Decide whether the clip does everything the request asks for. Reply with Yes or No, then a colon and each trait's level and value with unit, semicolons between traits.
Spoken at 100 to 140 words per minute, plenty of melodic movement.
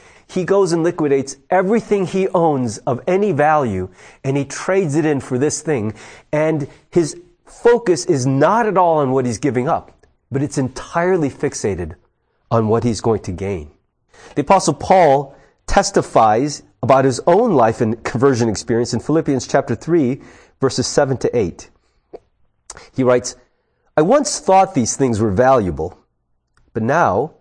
No: average, 155 wpm; wide, 6.3 semitones